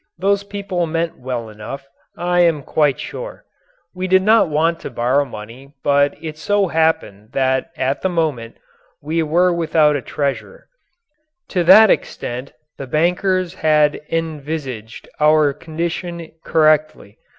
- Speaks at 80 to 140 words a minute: Yes, slow, 135 wpm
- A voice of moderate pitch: Yes, medium, 155 Hz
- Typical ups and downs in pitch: Yes, average, 4.0 semitones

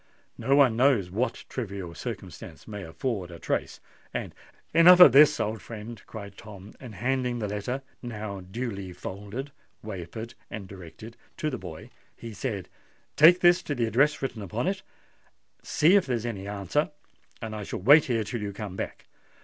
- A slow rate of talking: No, average, 170 wpm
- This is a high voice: No, low, 110 Hz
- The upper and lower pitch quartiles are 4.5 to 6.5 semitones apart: Yes, average, 4.8 semitones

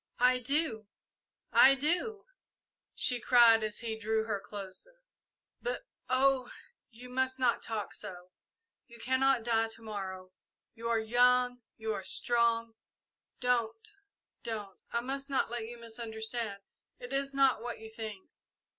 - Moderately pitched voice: No, high, 235 Hz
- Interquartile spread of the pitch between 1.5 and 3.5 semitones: Yes, average, 2.7 semitones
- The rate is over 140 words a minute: No, slow, 135 wpm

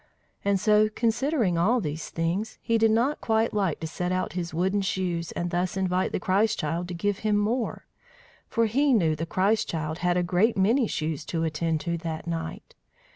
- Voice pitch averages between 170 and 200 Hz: Yes, medium, 185 Hz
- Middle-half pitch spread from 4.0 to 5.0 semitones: Yes, average, 4.5 semitones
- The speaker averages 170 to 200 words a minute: Yes, average, 195 wpm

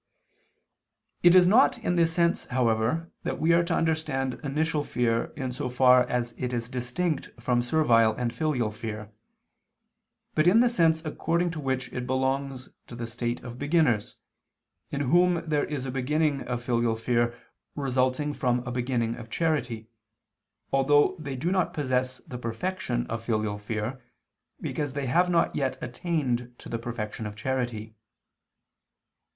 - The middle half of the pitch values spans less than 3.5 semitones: No, average, 4.6 semitones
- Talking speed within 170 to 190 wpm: No, average, 155 wpm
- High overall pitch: No, low, 130 Hz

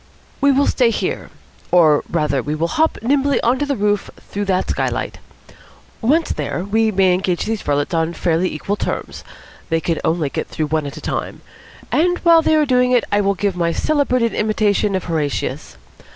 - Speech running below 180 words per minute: No, average, 195 wpm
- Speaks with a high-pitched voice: Yes, high, 200 Hz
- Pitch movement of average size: No, wide, 7.1 semitones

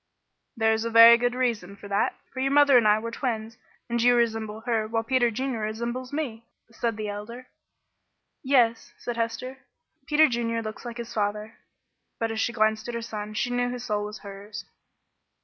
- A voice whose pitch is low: No, high, 230 Hz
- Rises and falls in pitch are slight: Yes, narrow, 2.2 semitones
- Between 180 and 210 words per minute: Yes, average, 190 wpm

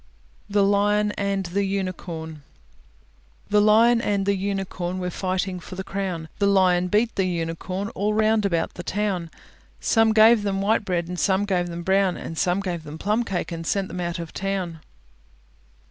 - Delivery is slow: No, average, 175 wpm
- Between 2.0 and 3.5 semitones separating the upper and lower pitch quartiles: Yes, narrow, 2.5 semitones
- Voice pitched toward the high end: Yes, high, 195 Hz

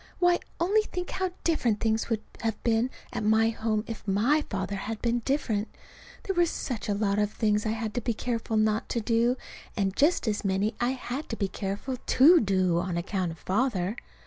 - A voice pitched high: Yes, high, 225 Hz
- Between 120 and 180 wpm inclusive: No, average, 200 wpm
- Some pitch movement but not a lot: Yes, average, 3.8 semitones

